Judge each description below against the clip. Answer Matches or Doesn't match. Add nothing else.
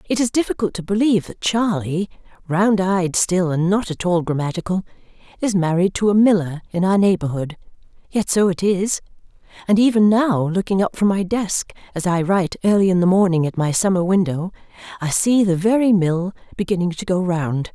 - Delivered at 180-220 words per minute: Matches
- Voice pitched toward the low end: Doesn't match